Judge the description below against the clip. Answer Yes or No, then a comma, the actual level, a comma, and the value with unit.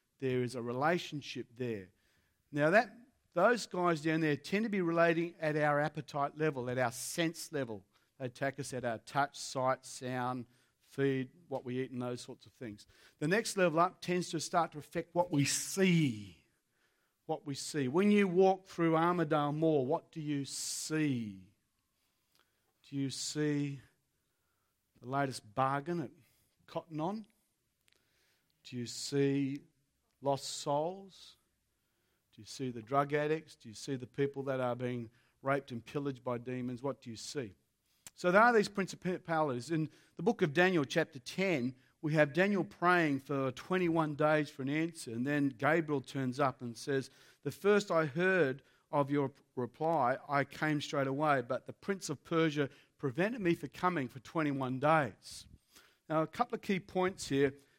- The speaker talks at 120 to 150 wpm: No, average, 165 wpm